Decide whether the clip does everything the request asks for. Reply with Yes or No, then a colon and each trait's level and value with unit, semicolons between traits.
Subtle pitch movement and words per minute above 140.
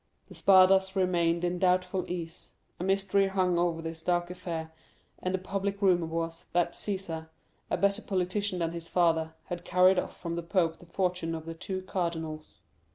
Yes: narrow, 2.2 semitones; average, 175 wpm